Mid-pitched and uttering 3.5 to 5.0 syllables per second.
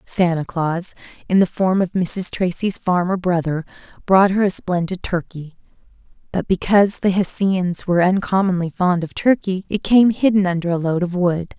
Yes: medium, 180 Hz; 4.8 syllables/s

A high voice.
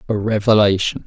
No: low, 105 Hz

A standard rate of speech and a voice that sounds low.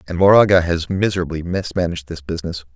Yes: average, 150 wpm; very low, 85 Hz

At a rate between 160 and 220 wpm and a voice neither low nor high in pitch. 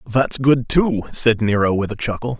No: average, 200 wpm; low, 120 Hz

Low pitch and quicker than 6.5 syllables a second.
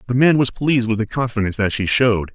Yes: low, 115 Hz; 6.9 syllables/s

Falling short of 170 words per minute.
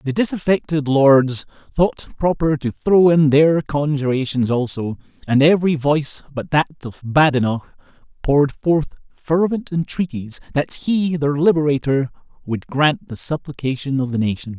Yes: slow, 135 wpm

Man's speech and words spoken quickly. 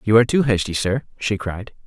Yes: male; fast, 225 wpm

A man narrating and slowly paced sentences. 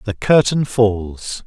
Yes: male; slow, 125 wpm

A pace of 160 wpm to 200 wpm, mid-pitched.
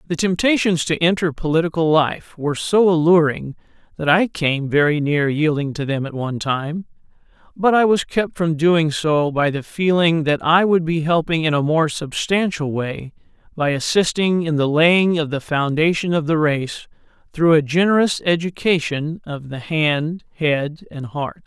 Yes: average, 170 wpm; medium, 160 Hz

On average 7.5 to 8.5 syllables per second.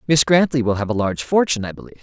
Yes: 8.2 syllables/s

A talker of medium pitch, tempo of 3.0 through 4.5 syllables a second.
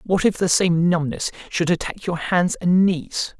Yes: medium, 175 Hz; 4.2 syllables/s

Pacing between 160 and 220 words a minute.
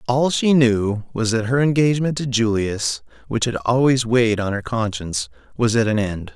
Yes: average, 190 wpm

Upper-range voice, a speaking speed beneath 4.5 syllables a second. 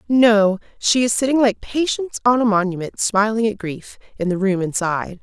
No: high, 215 Hz; 5.2 syllables/s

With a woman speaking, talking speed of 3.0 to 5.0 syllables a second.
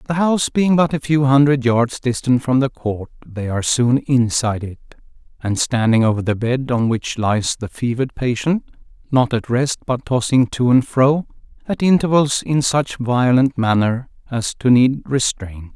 No: male; 4.6 syllables/s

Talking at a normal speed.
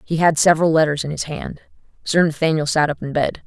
No: fast, 225 wpm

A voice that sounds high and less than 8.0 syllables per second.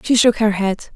Yes: high, 215 Hz; 5.3 syllables/s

